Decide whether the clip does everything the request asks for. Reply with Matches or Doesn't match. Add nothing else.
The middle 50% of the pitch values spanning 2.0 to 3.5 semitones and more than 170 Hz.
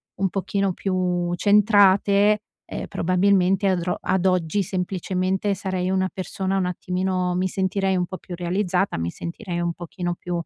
Doesn't match